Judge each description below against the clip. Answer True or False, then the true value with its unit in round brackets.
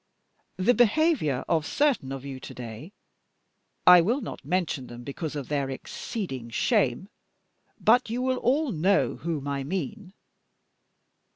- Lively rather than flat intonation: True (8.9 semitones)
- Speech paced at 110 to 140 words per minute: True (135 wpm)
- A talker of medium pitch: True (165 Hz)